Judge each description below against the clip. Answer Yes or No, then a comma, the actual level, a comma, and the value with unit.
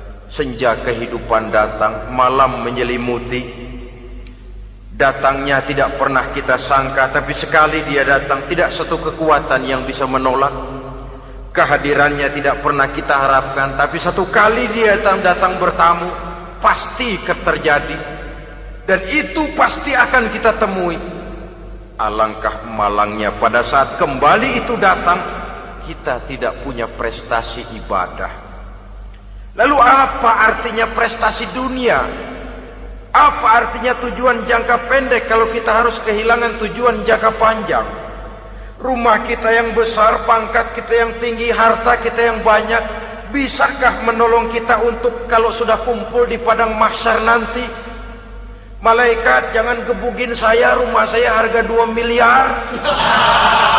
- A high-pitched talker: No, medium, 175 Hz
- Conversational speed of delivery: Yes, average, 115 wpm